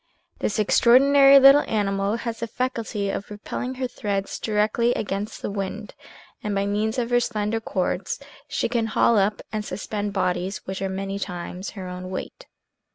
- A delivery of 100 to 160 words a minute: No, average, 170 wpm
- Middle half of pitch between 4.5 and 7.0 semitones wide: No, average, 3.0 semitones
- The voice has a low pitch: No, high, 210 Hz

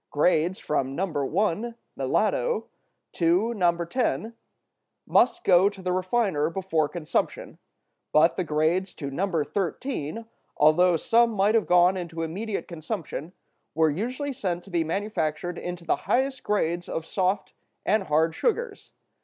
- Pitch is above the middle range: No, medium, 180 Hz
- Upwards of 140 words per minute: No, slow, 135 wpm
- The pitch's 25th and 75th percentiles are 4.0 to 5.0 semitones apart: Yes, average, 4.6 semitones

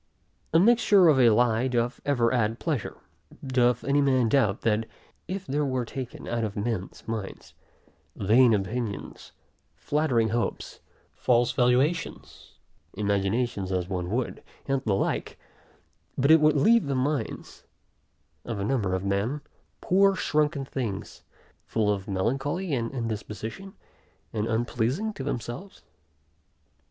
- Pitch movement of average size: Yes, average, 4.6 semitones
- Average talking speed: No, slow, 130 wpm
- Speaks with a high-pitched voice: No, low, 120 Hz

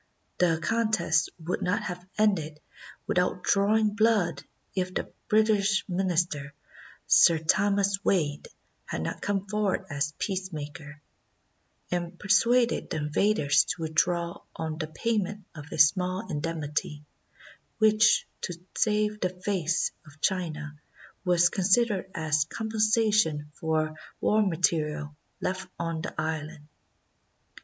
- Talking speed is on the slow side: Yes, slow, 115 wpm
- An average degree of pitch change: Yes, average, 4.6 semitones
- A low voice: No, medium, 180 Hz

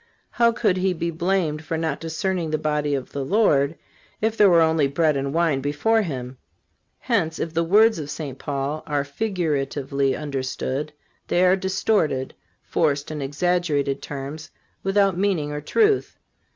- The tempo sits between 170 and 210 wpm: No, average, 155 wpm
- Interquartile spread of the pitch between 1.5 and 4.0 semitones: No, average, 4.6 semitones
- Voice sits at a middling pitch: Yes, medium, 155 Hz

